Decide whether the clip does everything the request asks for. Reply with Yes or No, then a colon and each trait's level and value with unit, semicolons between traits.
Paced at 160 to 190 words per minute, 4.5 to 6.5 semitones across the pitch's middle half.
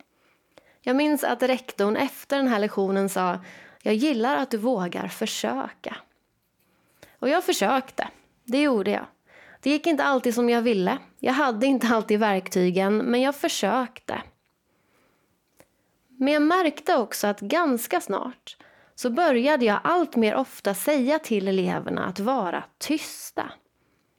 No: average, 135 wpm; wide, 5.5 semitones